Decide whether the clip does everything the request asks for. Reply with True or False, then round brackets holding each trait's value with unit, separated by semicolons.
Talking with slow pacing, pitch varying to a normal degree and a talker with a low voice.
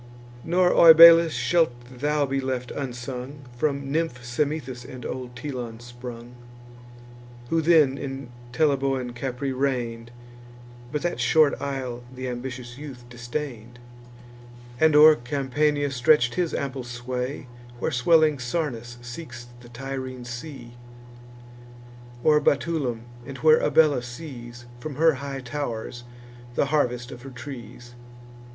True (120 wpm; 3.5 semitones; 130 Hz)